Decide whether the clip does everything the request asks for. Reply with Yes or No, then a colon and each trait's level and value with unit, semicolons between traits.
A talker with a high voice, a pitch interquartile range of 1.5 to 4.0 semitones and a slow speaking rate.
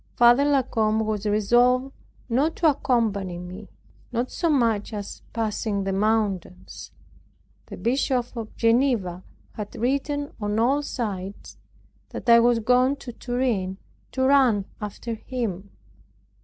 Yes: high, 230 Hz; average, 3.7 semitones; slow, 130 wpm